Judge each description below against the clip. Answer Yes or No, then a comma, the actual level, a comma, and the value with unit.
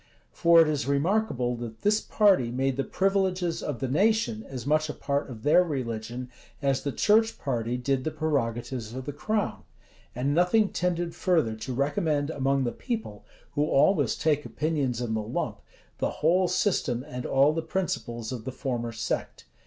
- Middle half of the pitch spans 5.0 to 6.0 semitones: Yes, wide, 5.5 semitones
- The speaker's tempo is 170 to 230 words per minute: Yes, average, 175 wpm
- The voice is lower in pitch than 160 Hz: Yes, medium, 140 Hz